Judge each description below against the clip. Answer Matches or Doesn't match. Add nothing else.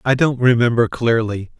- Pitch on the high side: Doesn't match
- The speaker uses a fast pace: Doesn't match